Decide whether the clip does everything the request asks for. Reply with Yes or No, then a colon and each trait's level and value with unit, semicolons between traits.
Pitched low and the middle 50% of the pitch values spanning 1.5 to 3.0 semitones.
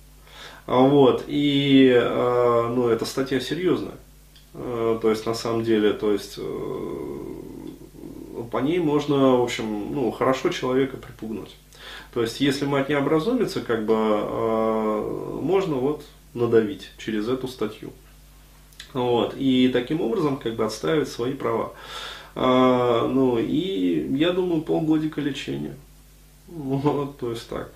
No: low, 130 Hz; average, 4.1 semitones